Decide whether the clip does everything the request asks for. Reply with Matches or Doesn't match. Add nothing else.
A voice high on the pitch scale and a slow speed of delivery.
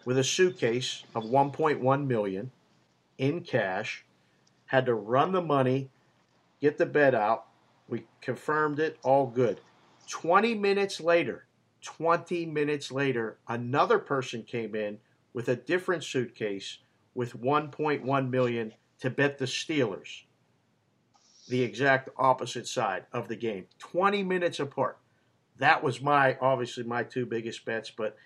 Doesn't match